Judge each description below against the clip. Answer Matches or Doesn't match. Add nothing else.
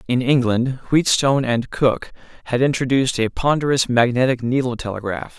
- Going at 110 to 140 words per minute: Matches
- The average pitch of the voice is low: Matches